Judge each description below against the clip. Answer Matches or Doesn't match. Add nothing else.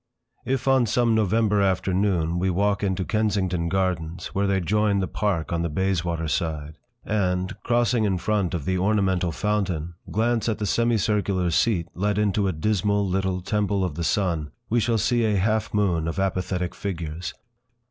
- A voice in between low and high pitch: Doesn't match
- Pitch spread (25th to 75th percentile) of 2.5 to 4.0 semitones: Matches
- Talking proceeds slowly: Doesn't match